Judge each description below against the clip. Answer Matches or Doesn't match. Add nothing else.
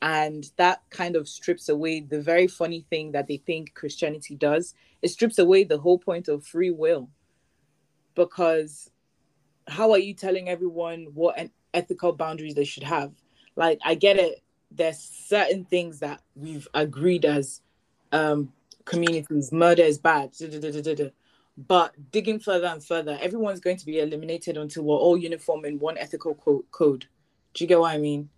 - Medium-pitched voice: Matches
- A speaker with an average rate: Matches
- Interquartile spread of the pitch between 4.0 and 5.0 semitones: Doesn't match